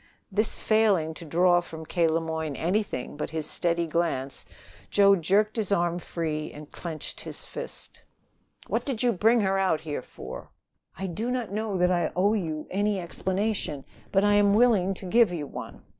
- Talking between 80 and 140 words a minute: No, average, 180 wpm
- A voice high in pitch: No, medium, 180 Hz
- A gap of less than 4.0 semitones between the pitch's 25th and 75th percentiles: No, average, 4.3 semitones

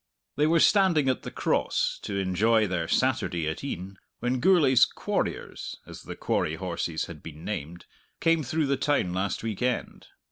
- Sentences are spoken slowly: No, average, 170 wpm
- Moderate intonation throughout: No, wide, 8.2 semitones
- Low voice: Yes, low, 110 Hz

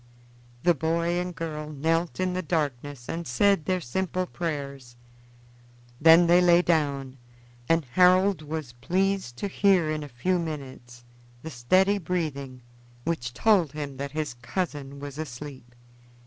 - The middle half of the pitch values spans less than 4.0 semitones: No, average, 4.5 semitones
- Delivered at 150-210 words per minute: No, average, 140 wpm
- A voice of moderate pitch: Yes, medium, 155 Hz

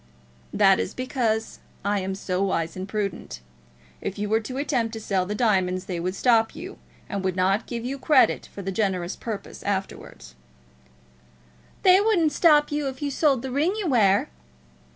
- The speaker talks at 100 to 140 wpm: No, average, 175 wpm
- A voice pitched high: Yes, high, 220 Hz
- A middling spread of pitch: No, wide, 6.1 semitones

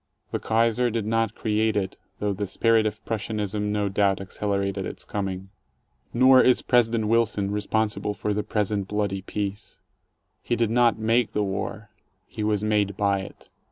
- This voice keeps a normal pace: Yes, average, 160 wpm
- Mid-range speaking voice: No, low, 105 Hz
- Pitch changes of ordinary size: No, narrow, 1.9 semitones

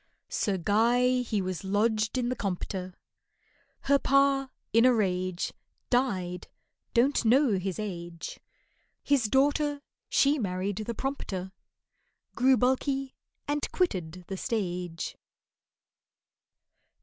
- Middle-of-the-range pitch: No, high, 220 Hz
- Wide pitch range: Yes, wide, 6.2 semitones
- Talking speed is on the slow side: Yes, slow, 105 wpm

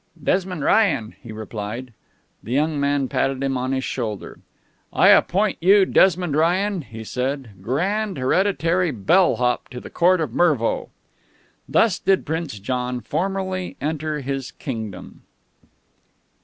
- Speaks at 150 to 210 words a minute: No, slow, 135 wpm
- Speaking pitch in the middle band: Yes, medium, 145 Hz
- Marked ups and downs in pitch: Yes, wide, 6.6 semitones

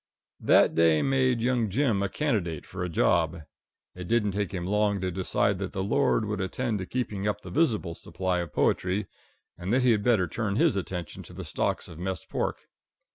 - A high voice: No, low, 100 Hz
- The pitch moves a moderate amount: Yes, average, 4.0 semitones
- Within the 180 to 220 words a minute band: Yes, average, 200 wpm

